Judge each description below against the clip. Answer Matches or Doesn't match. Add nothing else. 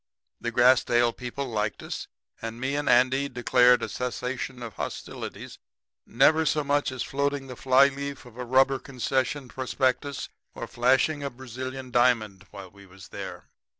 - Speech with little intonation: Matches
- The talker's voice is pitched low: Matches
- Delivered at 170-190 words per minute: Doesn't match